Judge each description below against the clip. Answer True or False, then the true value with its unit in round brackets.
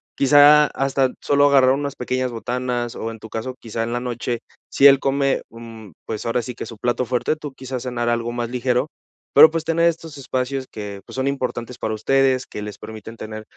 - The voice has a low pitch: True (125 Hz)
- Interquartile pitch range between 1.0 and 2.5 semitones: False (2.9 semitones)